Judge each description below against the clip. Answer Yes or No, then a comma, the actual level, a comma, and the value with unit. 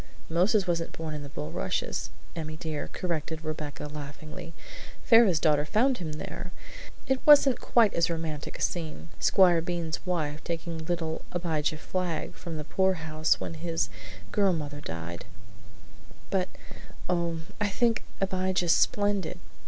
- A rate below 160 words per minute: Yes, slow, 135 wpm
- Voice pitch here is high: No, medium, 165 Hz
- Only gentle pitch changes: No, average, 3.1 semitones